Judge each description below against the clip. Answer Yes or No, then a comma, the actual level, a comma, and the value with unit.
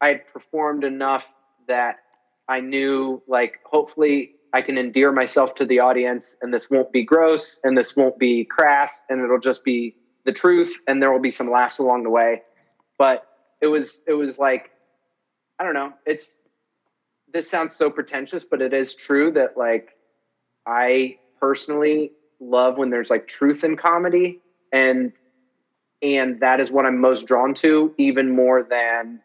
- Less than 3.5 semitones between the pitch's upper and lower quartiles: Yes, narrow, 2.6 semitones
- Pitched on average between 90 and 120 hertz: No, low, 130 Hz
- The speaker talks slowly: No, average, 170 wpm